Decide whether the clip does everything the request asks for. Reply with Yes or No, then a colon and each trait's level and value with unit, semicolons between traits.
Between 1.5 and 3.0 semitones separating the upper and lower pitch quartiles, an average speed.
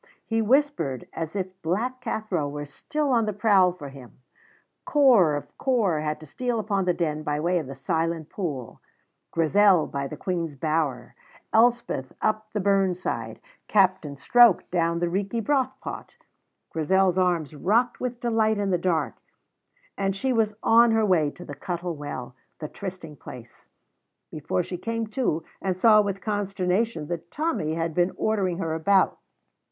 No: wide, 5.4 semitones; average, 160 wpm